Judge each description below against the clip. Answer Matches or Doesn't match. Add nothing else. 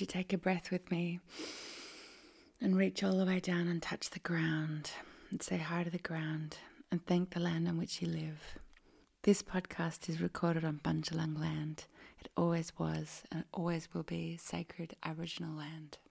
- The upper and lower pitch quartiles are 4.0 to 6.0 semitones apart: Doesn't match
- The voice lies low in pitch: Doesn't match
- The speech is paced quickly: Doesn't match